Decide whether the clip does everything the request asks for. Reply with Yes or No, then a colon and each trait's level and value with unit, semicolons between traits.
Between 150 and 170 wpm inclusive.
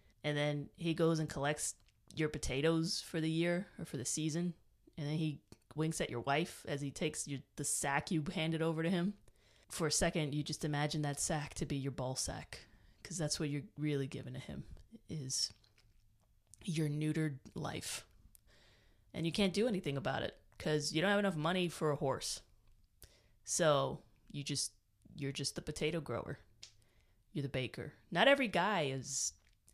No: average, 180 wpm